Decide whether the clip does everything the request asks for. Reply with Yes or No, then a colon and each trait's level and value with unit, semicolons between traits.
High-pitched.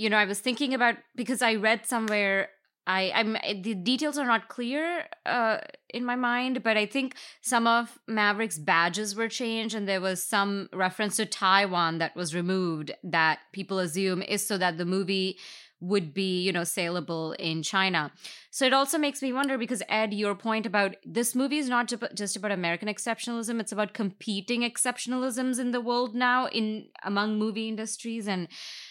Yes: high, 215 Hz